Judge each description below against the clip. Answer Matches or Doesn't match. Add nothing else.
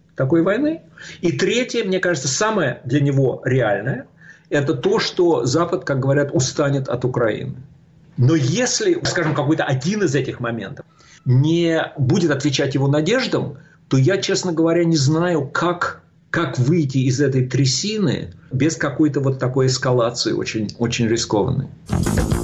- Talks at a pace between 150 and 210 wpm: Doesn't match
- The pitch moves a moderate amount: Matches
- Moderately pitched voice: Matches